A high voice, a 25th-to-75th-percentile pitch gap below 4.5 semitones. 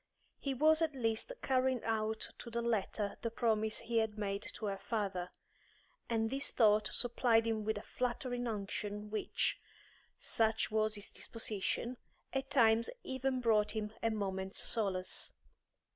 Yes: high, 225 Hz; narrow, 2.4 semitones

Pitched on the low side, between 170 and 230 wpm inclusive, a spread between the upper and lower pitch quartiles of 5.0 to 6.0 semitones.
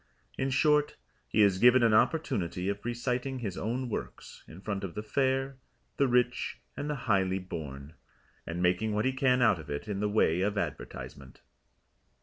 Yes: low, 110 Hz; average, 175 wpm; wide, 5.5 semitones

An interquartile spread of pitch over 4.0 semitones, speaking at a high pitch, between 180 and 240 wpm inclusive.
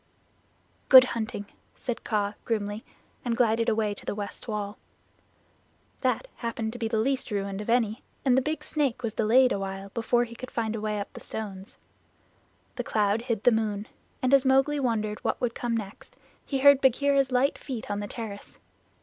No: average, 3.3 semitones; high, 230 Hz; average, 185 wpm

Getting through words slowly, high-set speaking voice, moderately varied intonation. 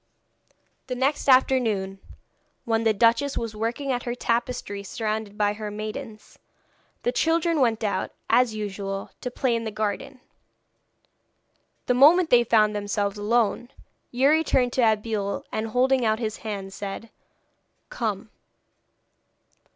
Yes: slow, 130 wpm; high, 225 Hz; average, 3.2 semitones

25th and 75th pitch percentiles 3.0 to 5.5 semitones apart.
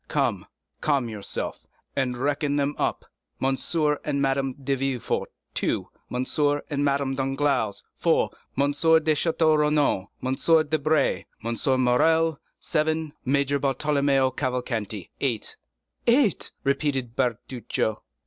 No: narrow, 2.6 semitones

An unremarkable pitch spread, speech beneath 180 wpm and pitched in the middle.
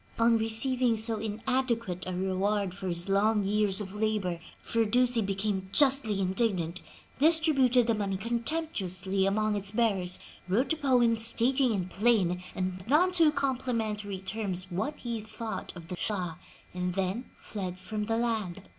No: average, 3.9 semitones; average, 145 wpm; high, 215 Hz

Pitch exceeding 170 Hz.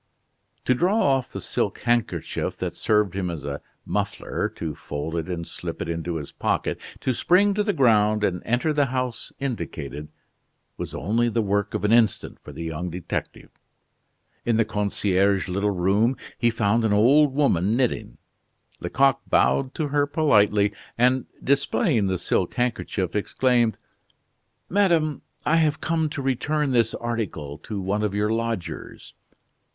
No: low, 115 Hz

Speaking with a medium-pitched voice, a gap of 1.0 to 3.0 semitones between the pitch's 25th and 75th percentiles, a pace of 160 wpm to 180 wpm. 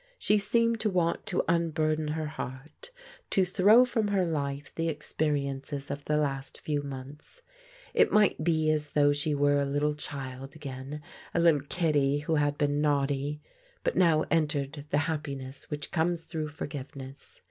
Yes: medium, 150 Hz; narrow, 2.5 semitones; average, 165 wpm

